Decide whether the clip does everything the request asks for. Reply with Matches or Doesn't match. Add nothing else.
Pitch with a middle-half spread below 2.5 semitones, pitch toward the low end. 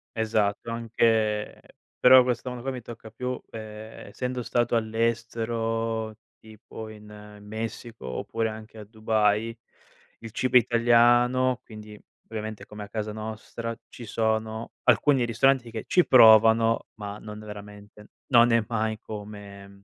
Matches